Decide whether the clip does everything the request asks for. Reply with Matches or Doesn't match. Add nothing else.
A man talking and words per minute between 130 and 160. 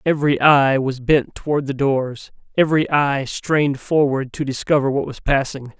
Matches